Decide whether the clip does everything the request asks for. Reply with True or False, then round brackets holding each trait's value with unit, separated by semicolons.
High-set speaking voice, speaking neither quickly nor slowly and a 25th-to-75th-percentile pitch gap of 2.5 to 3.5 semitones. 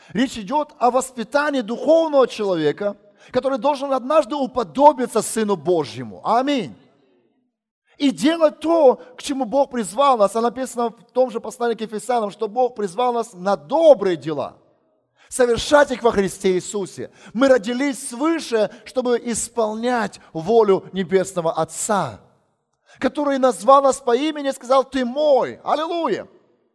False (240 Hz; 130 wpm; 4.6 semitones)